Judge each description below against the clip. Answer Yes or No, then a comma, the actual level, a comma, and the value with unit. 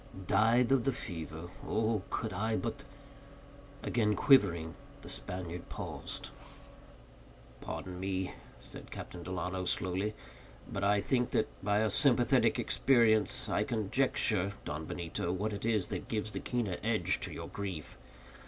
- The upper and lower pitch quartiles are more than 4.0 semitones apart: No, average, 3.7 semitones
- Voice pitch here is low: Yes, low, 105 Hz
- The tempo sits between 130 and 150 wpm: Yes, slow, 135 wpm